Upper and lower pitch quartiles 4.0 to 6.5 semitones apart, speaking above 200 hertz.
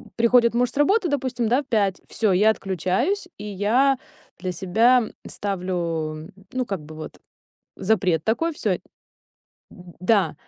Yes: wide, 5.5 semitones; high, 210 Hz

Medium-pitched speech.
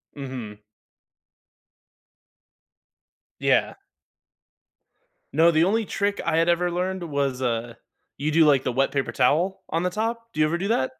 Yes: medium, 160 Hz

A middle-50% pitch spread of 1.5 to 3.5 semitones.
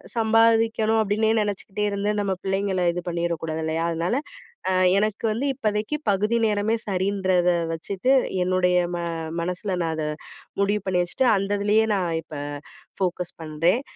Yes: average, 3.1 semitones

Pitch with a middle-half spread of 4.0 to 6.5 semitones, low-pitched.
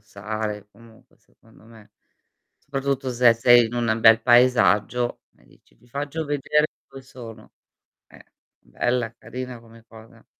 No: narrow, 2.4 semitones; low, 120 Hz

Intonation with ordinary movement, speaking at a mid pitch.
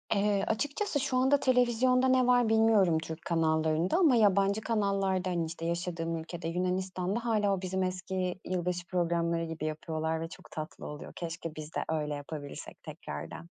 Yes: average, 4.6 semitones; medium, 180 Hz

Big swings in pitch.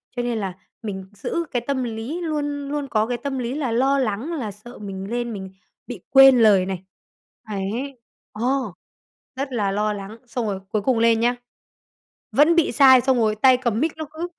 No: average, 4.4 semitones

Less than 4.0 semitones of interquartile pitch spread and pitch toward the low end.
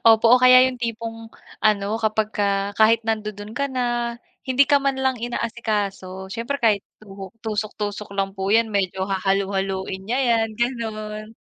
No: narrow, 2.5 semitones; high, 215 Hz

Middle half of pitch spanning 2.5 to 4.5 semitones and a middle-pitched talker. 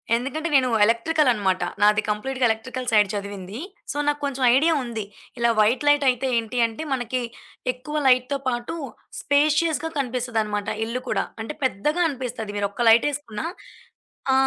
No: average, 4.2 semitones; very high, 250 Hz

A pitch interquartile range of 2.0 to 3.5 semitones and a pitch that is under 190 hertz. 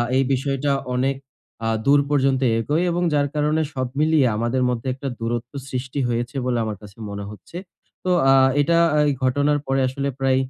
Yes: average, 3.0 semitones; low, 135 Hz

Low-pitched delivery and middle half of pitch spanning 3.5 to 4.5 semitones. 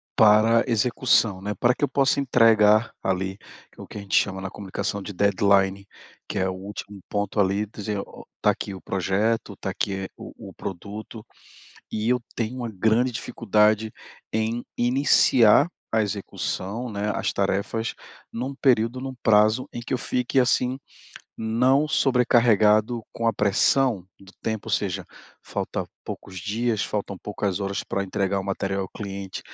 No: low, 105 Hz; average, 3.1 semitones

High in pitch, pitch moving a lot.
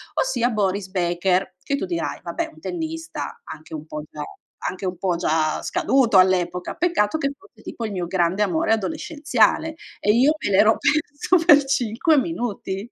Yes: high, 210 Hz; wide, 8.2 semitones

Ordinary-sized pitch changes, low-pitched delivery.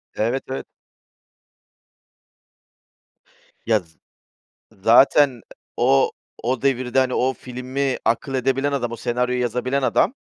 No: narrow, 2.0 semitones; low, 125 Hz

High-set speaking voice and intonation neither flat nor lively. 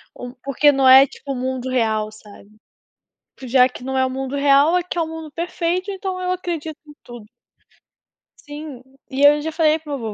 Yes: very high, 280 Hz; average, 3.8 semitones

